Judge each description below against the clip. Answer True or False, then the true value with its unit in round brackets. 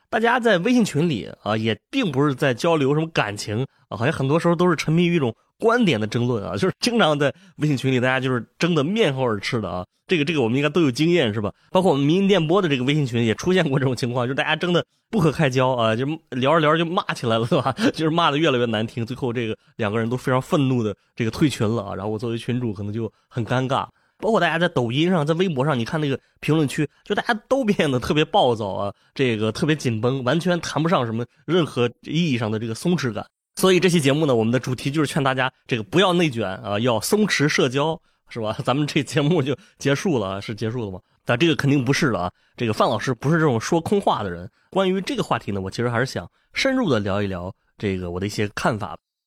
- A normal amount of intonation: False (6.4 semitones)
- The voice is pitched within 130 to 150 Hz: True (135 Hz)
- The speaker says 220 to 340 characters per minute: False (375 characters per minute)